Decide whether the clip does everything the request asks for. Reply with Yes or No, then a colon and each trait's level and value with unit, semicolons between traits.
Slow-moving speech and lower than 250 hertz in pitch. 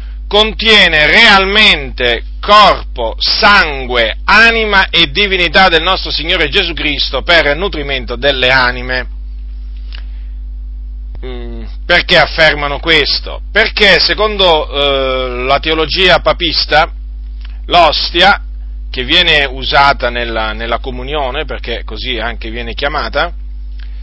Yes: slow, 90 wpm; low, 135 Hz